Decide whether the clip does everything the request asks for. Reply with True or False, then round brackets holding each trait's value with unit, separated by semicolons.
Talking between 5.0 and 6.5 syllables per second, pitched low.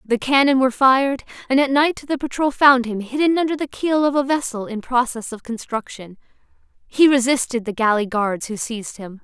False (5.4 syllables/s; 250 Hz)